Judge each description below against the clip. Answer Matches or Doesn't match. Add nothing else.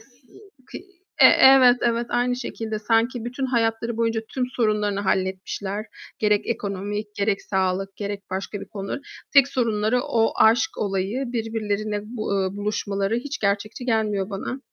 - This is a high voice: Matches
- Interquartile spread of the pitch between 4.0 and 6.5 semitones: Doesn't match